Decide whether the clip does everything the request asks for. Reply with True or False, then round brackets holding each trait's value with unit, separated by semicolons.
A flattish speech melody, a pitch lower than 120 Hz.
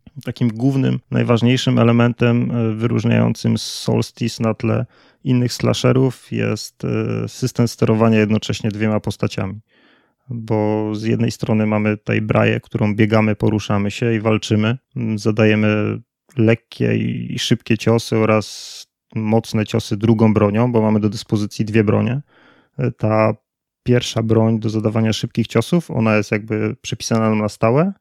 True (1.6 semitones; 110 Hz)